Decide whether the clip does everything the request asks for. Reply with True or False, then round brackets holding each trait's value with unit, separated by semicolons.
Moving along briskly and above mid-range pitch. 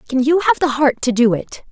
True (280 wpm; 260 Hz)